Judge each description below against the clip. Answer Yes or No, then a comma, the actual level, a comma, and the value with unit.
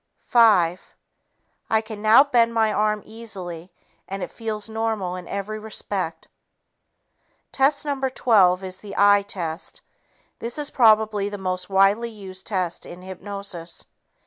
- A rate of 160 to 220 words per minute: No, slow, 135 wpm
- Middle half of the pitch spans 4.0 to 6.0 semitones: No, average, 3.1 semitones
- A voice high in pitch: Yes, high, 205 Hz